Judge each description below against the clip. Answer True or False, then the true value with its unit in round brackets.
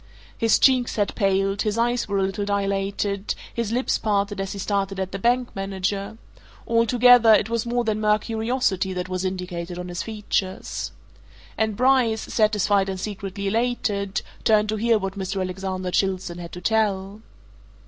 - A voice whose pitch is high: True (200 Hz)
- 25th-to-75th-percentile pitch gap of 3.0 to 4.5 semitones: False (2.6 semitones)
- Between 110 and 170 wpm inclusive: True (165 wpm)